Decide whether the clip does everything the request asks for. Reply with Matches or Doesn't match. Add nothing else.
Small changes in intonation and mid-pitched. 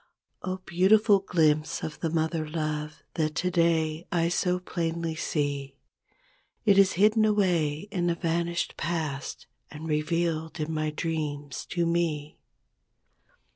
Matches